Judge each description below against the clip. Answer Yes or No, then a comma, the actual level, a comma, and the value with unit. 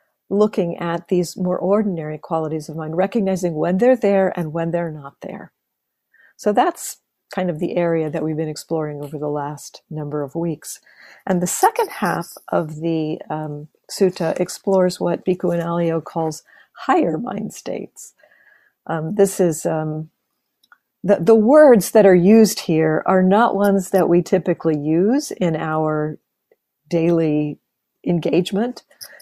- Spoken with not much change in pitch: No, average, 3.4 semitones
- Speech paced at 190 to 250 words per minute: No, average, 150 wpm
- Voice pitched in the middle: Yes, medium, 175 Hz